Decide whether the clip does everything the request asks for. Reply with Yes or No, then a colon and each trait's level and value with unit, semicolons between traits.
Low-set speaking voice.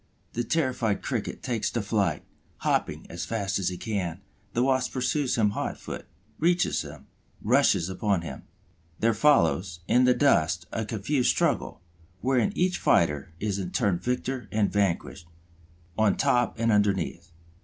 Yes: low, 110 Hz